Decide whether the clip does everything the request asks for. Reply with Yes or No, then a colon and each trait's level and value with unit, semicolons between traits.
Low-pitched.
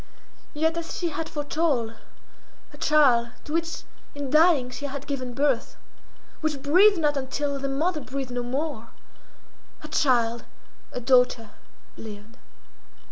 No: very high, 280 Hz